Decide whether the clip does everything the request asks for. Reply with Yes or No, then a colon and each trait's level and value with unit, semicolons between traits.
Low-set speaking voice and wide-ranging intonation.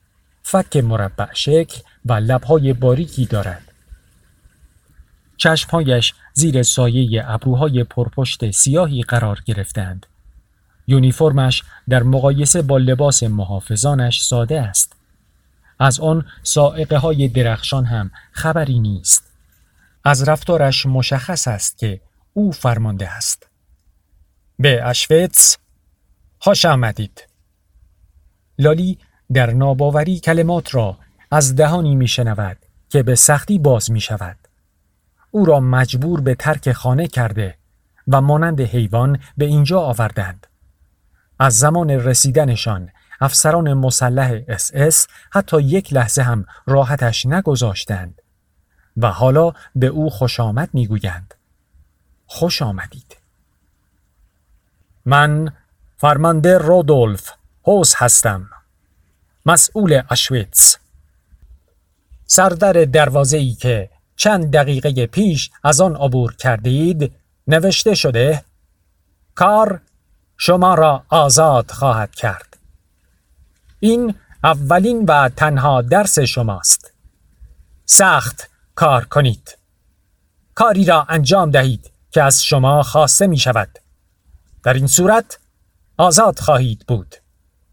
Yes: low, 125 Hz; wide, 8.2 semitones